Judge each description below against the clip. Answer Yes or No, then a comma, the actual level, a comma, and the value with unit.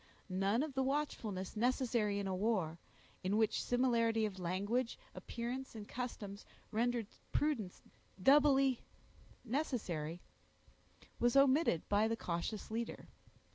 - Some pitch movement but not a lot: Yes, average, 4.3 semitones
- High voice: Yes, high, 230 Hz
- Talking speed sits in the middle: No, slow, 115 wpm